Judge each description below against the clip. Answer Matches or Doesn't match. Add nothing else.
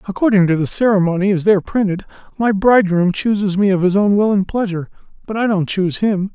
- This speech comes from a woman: Doesn't match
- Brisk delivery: Matches